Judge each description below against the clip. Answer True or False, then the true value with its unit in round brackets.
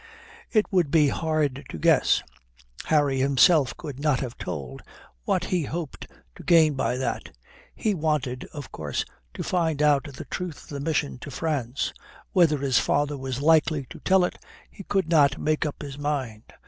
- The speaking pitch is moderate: True (145 Hz)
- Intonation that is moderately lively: True (3.3 semitones)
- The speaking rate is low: False (175 wpm)